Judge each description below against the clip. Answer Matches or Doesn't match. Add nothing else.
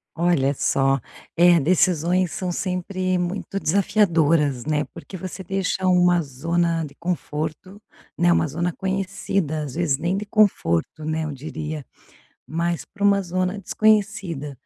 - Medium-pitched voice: Matches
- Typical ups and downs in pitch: Matches